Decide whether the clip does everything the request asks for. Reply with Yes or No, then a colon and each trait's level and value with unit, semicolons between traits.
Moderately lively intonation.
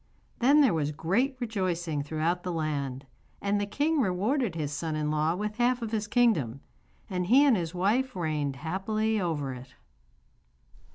No: wide, 6.3 semitones